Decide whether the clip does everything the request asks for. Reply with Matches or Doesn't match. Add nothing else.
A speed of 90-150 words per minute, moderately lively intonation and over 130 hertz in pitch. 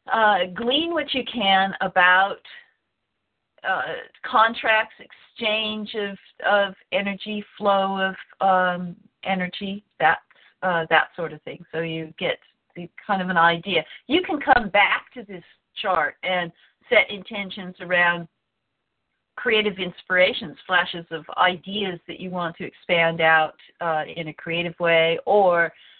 Matches